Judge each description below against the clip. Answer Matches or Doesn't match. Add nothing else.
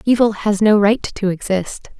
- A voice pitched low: Doesn't match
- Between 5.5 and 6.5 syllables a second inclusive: Doesn't match